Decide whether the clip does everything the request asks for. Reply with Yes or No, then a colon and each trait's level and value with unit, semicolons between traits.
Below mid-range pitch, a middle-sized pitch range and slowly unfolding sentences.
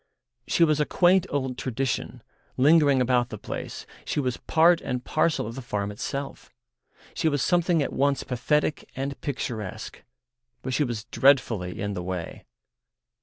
No: low, 130 Hz; average, 3.9 semitones; average, 150 wpm